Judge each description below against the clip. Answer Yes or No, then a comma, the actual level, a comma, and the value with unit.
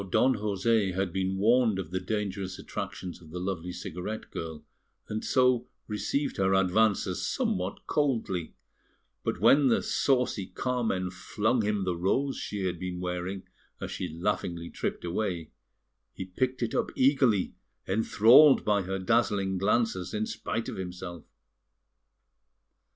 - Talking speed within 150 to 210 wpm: No, average, 140 wpm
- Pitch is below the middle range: Yes, very low, 95 Hz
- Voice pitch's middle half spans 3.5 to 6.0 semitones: Yes, average, 3.8 semitones